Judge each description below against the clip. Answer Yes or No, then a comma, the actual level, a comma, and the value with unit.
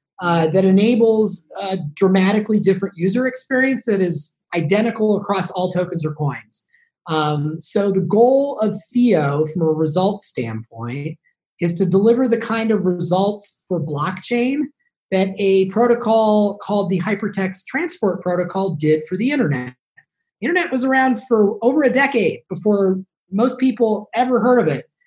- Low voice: No, high, 200 Hz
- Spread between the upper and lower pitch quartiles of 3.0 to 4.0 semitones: No, average, 4.8 semitones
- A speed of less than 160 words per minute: Yes, average, 145 wpm